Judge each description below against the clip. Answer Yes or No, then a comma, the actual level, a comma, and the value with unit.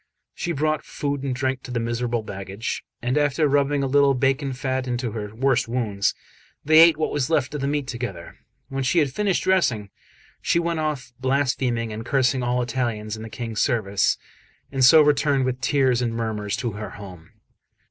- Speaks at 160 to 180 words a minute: No, average, 190 wpm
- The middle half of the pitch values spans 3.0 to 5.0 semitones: Yes, average, 3.6 semitones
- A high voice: No, low, 130 Hz